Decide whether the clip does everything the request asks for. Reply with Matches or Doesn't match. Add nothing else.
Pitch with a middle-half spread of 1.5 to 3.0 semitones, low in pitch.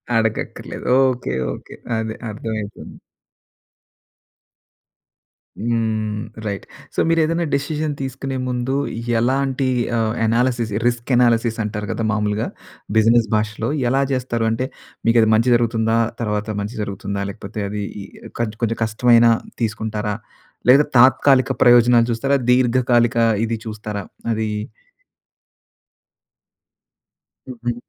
Matches